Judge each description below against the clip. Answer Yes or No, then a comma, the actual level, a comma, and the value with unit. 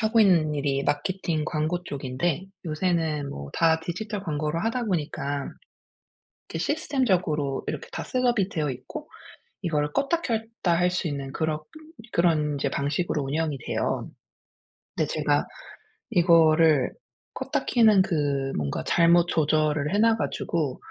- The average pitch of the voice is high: No, medium, 160 Hz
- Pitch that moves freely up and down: No, average, 4.1 semitones